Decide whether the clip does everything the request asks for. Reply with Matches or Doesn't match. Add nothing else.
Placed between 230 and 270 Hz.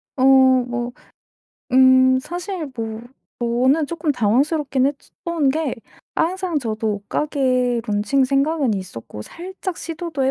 Matches